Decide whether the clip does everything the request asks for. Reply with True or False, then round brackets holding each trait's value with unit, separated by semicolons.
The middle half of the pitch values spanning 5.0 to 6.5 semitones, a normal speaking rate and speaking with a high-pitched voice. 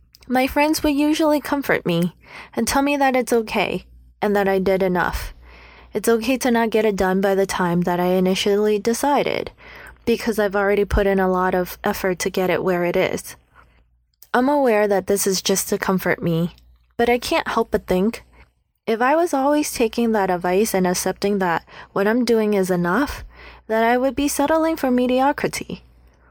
True (5.5 semitones; 190 wpm; 205 Hz)